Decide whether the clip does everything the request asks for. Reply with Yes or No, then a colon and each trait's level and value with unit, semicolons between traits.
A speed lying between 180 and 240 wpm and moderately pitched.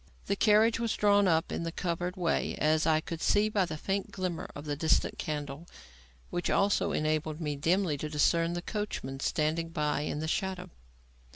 Yes: average, 190 wpm; medium, 165 Hz